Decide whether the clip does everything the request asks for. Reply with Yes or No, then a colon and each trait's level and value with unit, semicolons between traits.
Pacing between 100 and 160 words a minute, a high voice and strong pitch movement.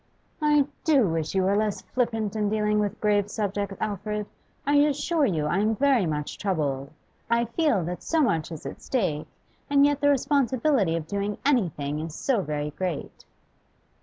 No: average, 170 wpm; high, 210 Hz; wide, 7.5 semitones